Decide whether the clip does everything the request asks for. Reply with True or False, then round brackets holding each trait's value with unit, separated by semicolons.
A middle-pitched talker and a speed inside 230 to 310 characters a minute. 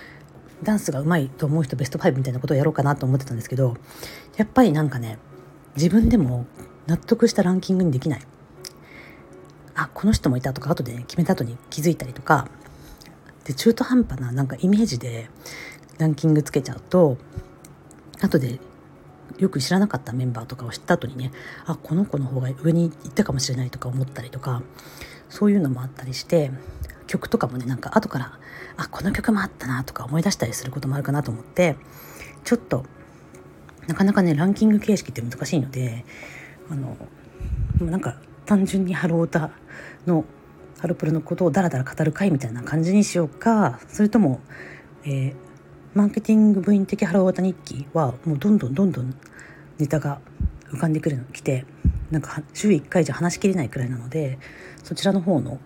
False (150 Hz; 370 characters per minute)